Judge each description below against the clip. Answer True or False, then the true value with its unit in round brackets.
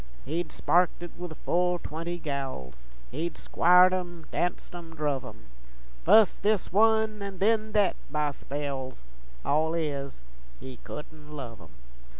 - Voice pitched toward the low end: False (165 Hz)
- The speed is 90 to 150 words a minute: True (140 wpm)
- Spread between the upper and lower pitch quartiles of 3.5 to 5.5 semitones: True (4.2 semitones)